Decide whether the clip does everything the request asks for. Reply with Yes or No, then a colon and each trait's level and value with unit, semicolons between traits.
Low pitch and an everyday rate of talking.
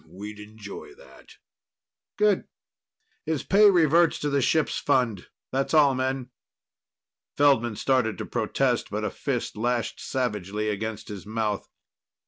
No: low, 125 Hz; slow, 125 wpm